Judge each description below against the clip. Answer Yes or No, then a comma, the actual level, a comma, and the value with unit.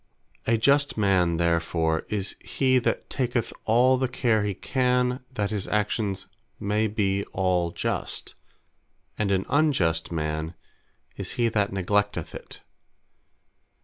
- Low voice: Yes, low, 105 Hz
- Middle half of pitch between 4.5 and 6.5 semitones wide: Yes, average, 5.1 semitones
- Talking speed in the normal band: No, slow, 125 wpm